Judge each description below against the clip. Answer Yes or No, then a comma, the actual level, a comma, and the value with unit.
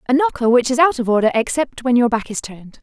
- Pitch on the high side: Yes, high, 245 Hz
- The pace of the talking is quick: Yes, fast, 275 wpm